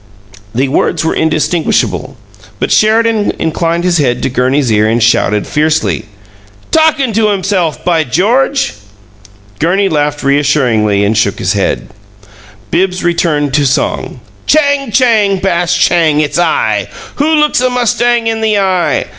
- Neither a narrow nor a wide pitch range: No, wide, 7.3 semitones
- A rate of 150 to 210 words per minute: No, average, 140 wpm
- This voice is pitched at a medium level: Yes, medium, 170 Hz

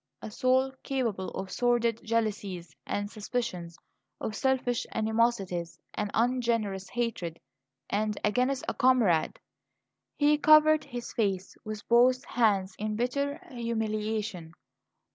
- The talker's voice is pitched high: Yes, high, 225 Hz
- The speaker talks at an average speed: No, slow, 110 wpm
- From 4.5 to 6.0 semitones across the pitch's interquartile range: No, average, 3.5 semitones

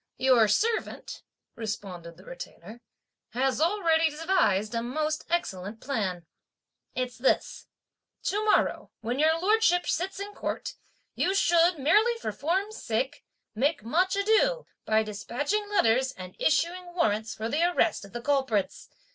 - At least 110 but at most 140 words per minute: Yes, slow, 135 wpm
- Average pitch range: No, wide, 8.5 semitones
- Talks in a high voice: Yes, very high, 285 Hz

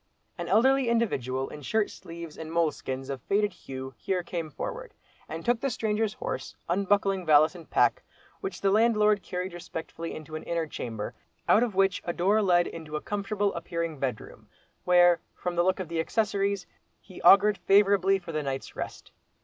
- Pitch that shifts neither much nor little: Yes, average, 4.2 semitones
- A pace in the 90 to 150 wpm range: No, average, 175 wpm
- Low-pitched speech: No, medium, 180 Hz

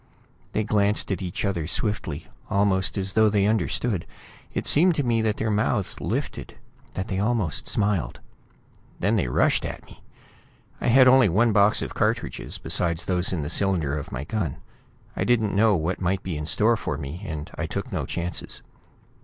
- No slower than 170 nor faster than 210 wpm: Yes, average, 180 wpm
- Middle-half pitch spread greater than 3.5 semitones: Yes, average, 4.0 semitones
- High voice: No, low, 100 Hz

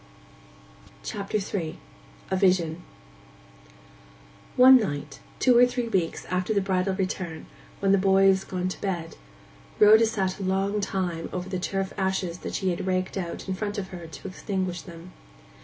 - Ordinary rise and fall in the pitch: No, narrow, 1.9 semitones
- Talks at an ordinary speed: Yes, average, 155 wpm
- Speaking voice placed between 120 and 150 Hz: No, high, 190 Hz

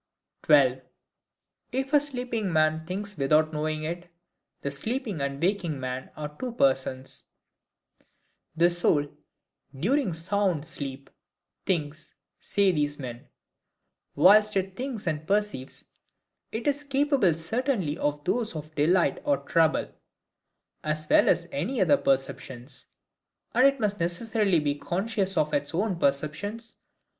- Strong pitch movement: Yes, wide, 6.3 semitones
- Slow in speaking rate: Yes, slow, 125 wpm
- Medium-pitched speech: Yes, medium, 170 Hz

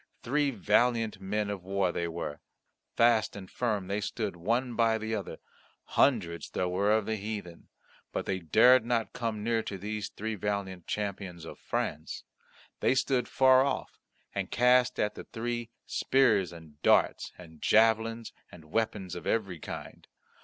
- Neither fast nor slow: Yes, average, 160 wpm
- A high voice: No, low, 105 Hz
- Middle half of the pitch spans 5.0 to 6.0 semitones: No, average, 3.8 semitones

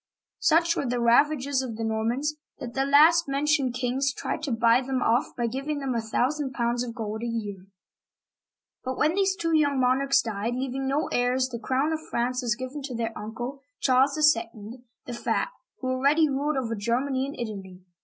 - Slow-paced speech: No, average, 190 wpm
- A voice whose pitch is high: Yes, very high, 255 Hz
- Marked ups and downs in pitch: No, average, 3.2 semitones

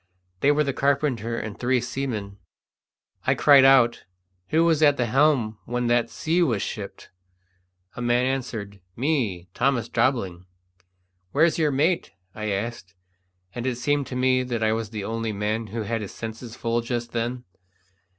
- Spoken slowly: No, average, 160 wpm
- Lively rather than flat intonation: No, average, 3.4 semitones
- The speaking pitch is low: Yes, low, 120 Hz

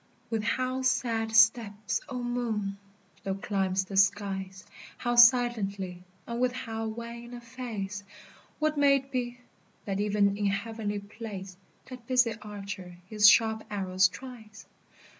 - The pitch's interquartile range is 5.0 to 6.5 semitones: No, average, 3.4 semitones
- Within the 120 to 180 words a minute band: Yes, slow, 135 wpm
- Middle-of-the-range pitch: No, high, 220 Hz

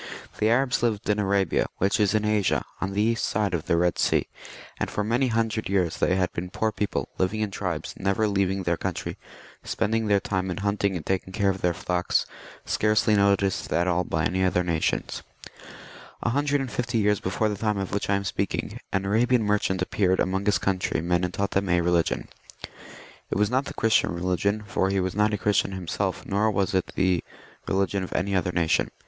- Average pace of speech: No, fast, 210 wpm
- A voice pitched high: No, low, 100 Hz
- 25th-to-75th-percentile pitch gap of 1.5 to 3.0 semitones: Yes, narrow, 2.5 semitones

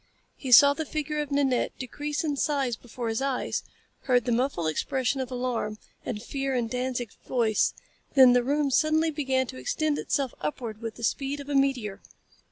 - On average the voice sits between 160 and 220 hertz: No, very high, 260 Hz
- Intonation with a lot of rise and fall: No, average, 3.0 semitones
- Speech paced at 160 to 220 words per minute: Yes, average, 180 wpm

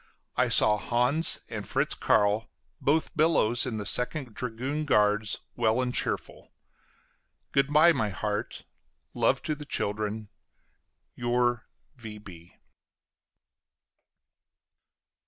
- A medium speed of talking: No, slow, 100 wpm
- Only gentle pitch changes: No, average, 4.5 semitones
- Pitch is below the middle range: Yes, low, 120 Hz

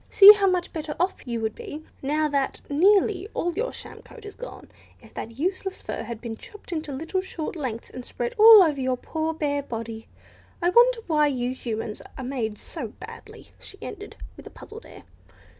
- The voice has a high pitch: Yes, very high, 310 Hz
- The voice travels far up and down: Yes, wide, 7.1 semitones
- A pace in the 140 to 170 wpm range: No, average, 195 wpm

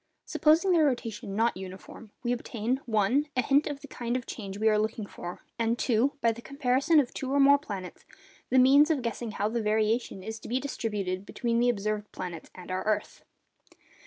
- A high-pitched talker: Yes, high, 230 Hz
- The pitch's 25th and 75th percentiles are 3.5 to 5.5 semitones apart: Yes, average, 4.0 semitones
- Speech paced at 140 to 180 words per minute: No, average, 195 wpm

